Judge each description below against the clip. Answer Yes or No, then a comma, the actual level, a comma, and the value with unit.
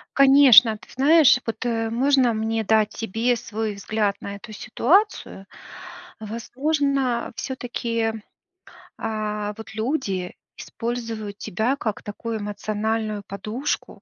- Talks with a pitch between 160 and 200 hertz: No, high, 225 Hz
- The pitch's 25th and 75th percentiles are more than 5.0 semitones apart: No, average, 2.7 semitones